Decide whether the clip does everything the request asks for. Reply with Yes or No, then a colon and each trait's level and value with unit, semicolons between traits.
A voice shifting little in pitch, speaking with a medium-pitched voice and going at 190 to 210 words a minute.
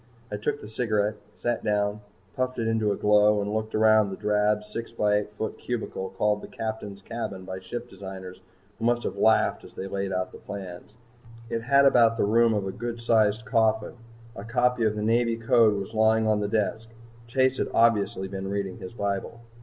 No: narrow, 2.2 semitones; low, 110 Hz; average, 200 wpm